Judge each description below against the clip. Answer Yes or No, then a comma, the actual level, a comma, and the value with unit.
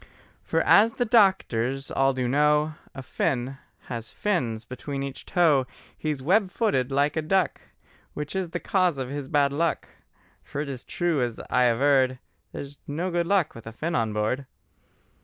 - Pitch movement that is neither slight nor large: Yes, average, 4.8 semitones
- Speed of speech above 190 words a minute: No, average, 175 wpm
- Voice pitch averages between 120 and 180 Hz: Yes, medium, 140 Hz